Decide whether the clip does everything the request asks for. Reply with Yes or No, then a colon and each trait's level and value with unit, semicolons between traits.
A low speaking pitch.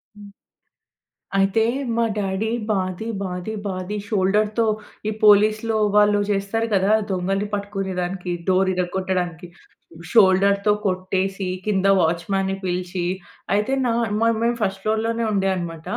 No: high, 195 Hz